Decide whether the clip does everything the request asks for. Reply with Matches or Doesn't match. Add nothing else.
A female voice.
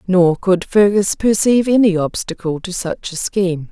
Matches